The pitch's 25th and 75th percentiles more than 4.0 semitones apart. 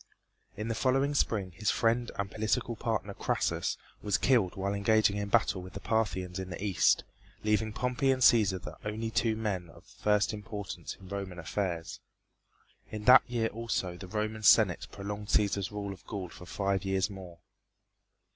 No: narrow, 2.6 semitones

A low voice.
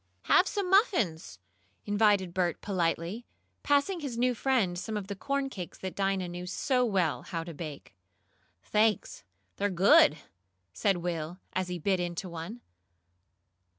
No: high, 190 Hz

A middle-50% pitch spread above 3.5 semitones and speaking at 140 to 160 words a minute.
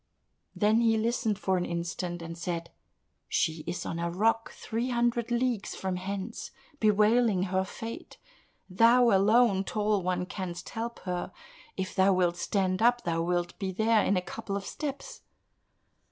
Yes: average, 3.9 semitones; average, 155 wpm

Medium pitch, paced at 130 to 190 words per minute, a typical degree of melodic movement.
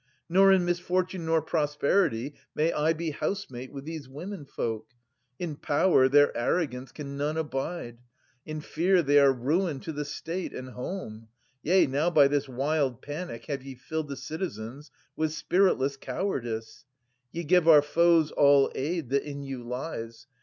Yes: medium, 145 Hz; average, 160 wpm; average, 3.9 semitones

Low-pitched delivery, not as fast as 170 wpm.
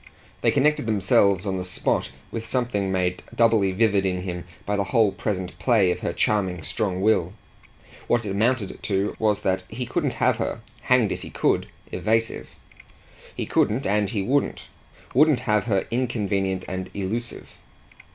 Yes: low, 105 Hz; average, 160 wpm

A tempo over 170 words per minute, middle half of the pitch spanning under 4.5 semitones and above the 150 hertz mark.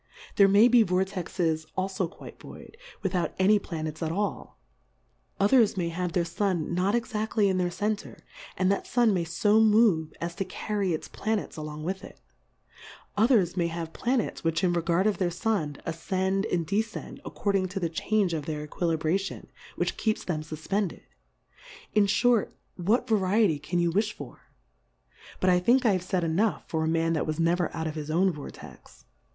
Yes: average, 180 wpm; average, 3.8 semitones; medium, 185 Hz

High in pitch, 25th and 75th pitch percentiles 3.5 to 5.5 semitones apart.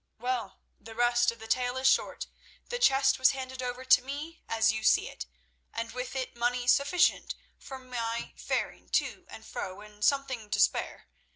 No: very high, 250 Hz; narrow, 2.4 semitones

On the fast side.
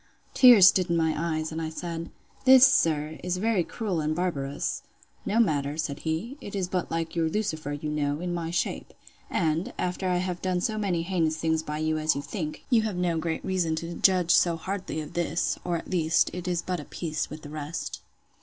Yes: fast, 215 wpm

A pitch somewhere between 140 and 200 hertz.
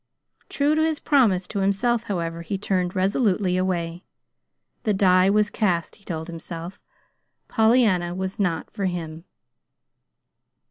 Yes: high, 190 Hz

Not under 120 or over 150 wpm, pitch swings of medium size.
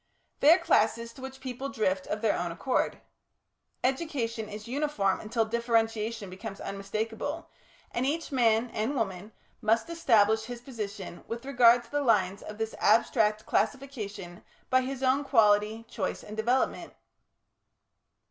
Yes: average, 140 wpm; average, 3.5 semitones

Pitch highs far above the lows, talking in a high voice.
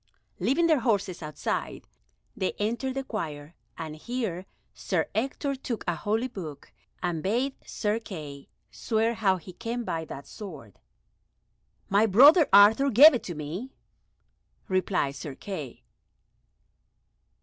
Yes: wide, 6.8 semitones; high, 205 Hz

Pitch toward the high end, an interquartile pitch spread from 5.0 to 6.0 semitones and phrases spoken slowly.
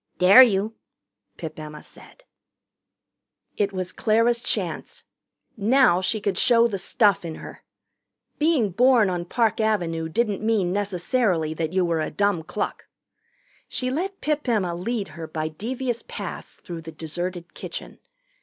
No: high, 200 Hz; wide, 5.4 semitones; average, 145 wpm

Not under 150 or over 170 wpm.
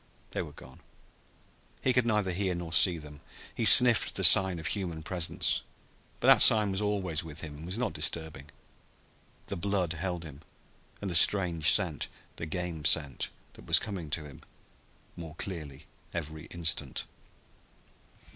Yes: average, 155 wpm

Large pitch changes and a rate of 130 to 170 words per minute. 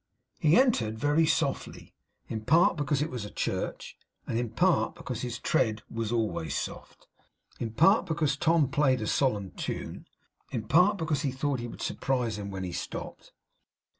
Yes: wide, 6.0 semitones; average, 165 wpm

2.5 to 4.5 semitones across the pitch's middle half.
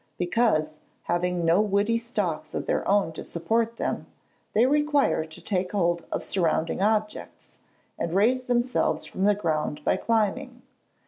No: average, 5.3 semitones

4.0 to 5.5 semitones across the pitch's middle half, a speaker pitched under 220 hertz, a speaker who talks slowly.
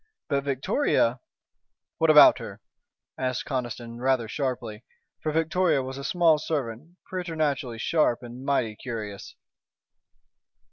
Yes: average, 4.7 semitones; low, 135 Hz; slow, 120 wpm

